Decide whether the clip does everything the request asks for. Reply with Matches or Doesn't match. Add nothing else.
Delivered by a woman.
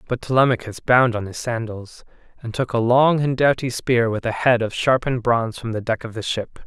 Doesn't match